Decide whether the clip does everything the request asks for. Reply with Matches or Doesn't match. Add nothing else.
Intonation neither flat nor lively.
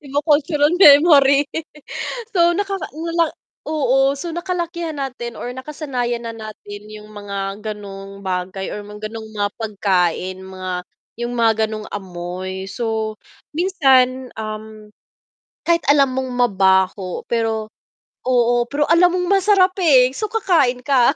Doesn't match